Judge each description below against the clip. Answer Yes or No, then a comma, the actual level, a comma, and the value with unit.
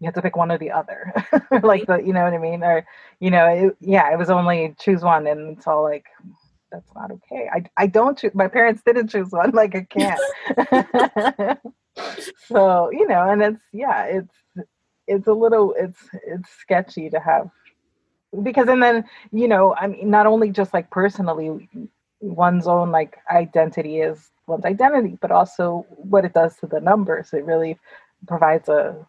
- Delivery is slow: No, average, 185 wpm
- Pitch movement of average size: Yes, average, 4.4 semitones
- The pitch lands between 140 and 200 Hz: Yes, high, 190 Hz